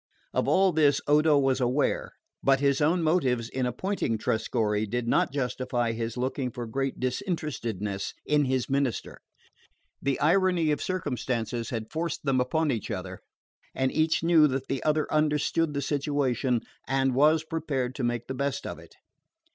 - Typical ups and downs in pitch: Yes, average, 3.6 semitones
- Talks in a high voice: No, low, 135 Hz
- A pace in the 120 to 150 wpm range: No, average, 160 wpm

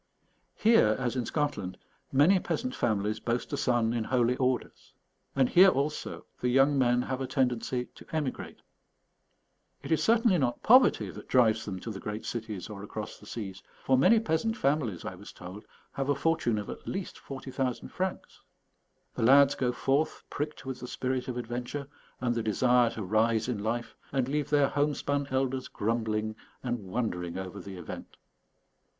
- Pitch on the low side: Yes, low, 125 Hz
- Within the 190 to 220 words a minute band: No, average, 170 wpm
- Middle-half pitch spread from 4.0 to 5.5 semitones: Yes, average, 4.3 semitones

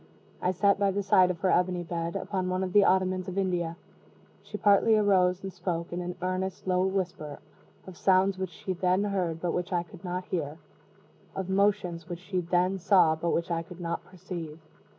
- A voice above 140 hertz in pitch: Yes, medium, 185 Hz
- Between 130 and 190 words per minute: No, average, 200 wpm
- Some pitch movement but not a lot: No, narrow, 1.6 semitones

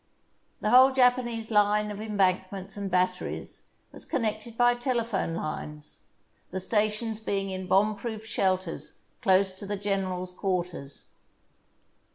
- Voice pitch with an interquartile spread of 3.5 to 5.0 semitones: No, average, 2.9 semitones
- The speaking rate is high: No, slow, 135 wpm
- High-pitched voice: Yes, high, 205 Hz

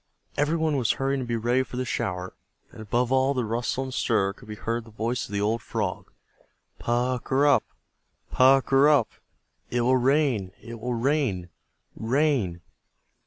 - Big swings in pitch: No, average, 3.3 semitones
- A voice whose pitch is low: Yes, low, 125 Hz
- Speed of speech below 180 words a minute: No, average, 185 wpm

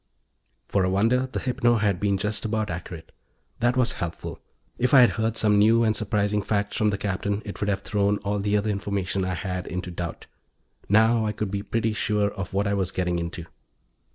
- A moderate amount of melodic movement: No, narrow, 2.2 semitones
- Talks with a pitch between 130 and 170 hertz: No, low, 105 Hz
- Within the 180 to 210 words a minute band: Yes, fast, 205 wpm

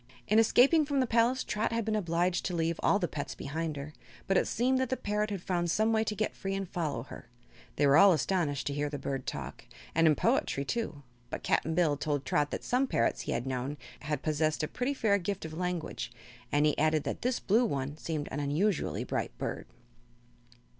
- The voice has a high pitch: No, medium, 170 Hz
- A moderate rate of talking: No, fast, 220 wpm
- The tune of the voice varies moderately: No, wide, 6.5 semitones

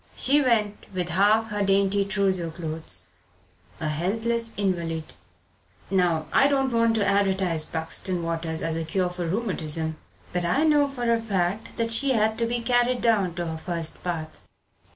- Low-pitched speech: No, high, 195 Hz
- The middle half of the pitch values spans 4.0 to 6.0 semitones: Yes, wide, 5.4 semitones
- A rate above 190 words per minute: No, average, 165 wpm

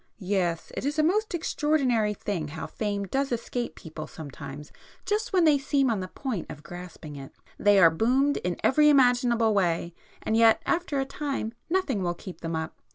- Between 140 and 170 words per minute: No, average, 180 wpm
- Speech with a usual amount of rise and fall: No, wide, 8.1 semitones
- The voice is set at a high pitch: Yes, high, 220 Hz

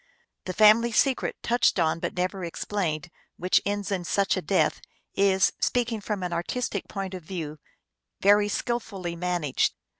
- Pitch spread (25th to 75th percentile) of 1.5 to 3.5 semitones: Yes, average, 3.0 semitones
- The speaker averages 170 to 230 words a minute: No, average, 155 wpm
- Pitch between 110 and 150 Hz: No, high, 190 Hz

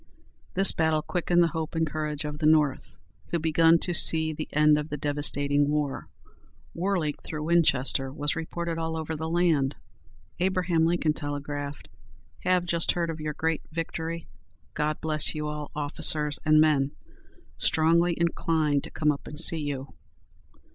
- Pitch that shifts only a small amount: Yes, narrow, 1.8 semitones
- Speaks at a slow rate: No, average, 155 wpm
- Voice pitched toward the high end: No, medium, 155 Hz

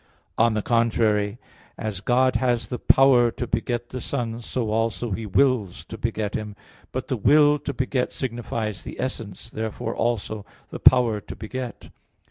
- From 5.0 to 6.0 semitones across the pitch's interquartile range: No, narrow, 2.6 semitones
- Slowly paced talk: No, average, 160 wpm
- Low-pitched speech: Yes, low, 115 Hz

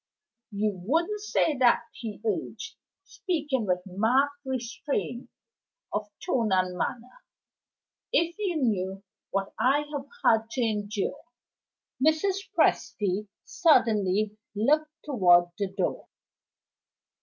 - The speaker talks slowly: Yes, slow, 110 wpm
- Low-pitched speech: No, high, 235 Hz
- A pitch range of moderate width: No, wide, 6.7 semitones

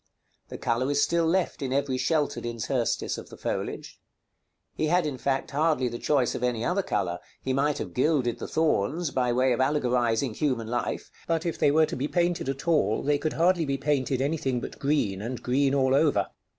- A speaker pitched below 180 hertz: Yes, low, 135 Hz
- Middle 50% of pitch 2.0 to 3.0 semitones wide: No, average, 3.7 semitones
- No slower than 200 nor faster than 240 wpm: Yes, fast, 205 wpm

